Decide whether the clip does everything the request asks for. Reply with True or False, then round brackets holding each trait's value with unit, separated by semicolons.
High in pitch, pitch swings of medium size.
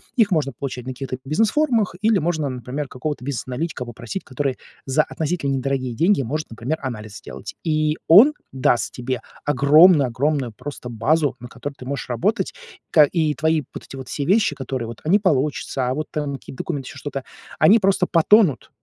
False (145 Hz; 4.0 semitones)